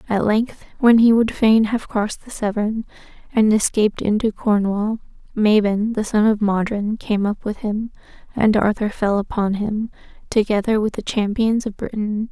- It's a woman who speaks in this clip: Yes, female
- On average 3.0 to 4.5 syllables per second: No, 4.7 syllables/s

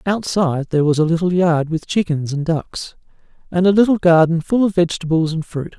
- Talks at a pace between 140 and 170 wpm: No, average, 195 wpm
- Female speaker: No, male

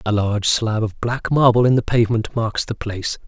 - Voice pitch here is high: No, low, 110 Hz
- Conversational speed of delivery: No, fast, 220 wpm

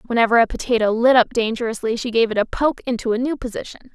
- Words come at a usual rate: No, fast, 230 wpm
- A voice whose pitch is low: No, high, 235 Hz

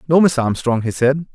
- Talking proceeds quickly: Yes, fast, 225 wpm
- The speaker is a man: Yes, male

